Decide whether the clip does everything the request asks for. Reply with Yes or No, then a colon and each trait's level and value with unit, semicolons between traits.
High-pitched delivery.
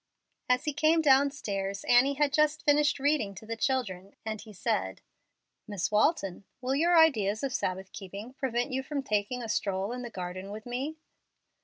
Yes: high, 245 Hz